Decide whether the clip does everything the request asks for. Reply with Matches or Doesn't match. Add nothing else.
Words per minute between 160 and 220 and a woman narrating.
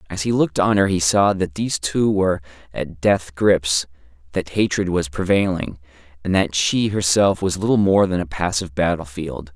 Doesn't match